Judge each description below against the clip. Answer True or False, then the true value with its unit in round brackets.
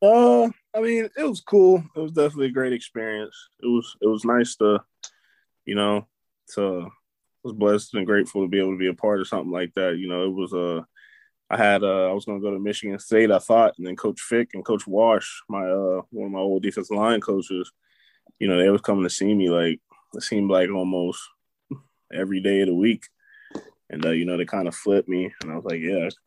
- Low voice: True (100 Hz)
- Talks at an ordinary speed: False (235 wpm)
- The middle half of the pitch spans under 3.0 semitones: False (3.8 semitones)